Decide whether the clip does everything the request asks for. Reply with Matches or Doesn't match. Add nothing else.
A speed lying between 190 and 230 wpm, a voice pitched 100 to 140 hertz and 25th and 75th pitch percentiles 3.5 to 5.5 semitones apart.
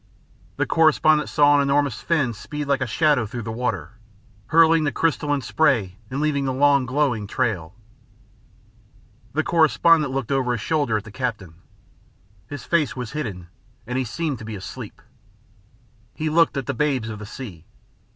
Doesn't match